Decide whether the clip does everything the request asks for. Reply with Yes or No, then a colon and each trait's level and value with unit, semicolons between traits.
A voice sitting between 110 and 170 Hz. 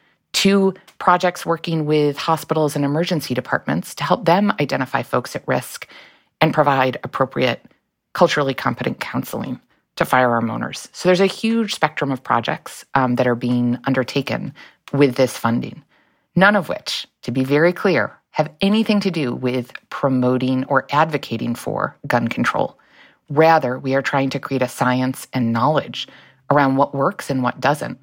Yes: medium, 140 Hz